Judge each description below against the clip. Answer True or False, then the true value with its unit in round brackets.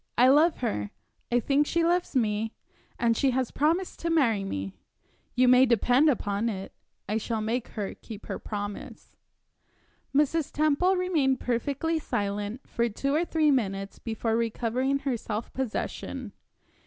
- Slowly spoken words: False (150 wpm)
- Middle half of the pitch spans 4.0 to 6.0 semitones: True (5.1 semitones)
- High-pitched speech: True (245 Hz)